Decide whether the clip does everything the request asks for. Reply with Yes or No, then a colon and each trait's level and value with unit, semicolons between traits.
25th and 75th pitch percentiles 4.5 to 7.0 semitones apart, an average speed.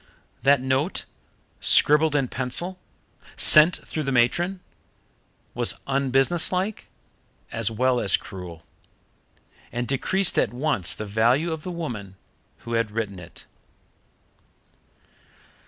No: wide, 5.6 semitones; slow, 105 wpm